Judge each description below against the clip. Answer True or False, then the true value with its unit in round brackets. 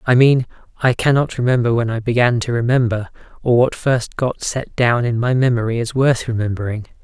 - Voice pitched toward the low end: True (120 Hz)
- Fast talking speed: False (190 wpm)